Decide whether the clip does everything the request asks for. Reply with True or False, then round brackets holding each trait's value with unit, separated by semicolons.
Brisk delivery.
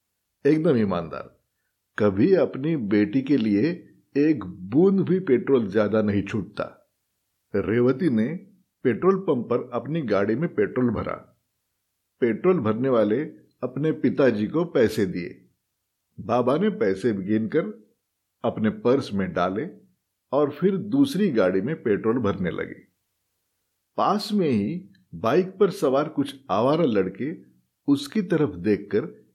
False (125 wpm)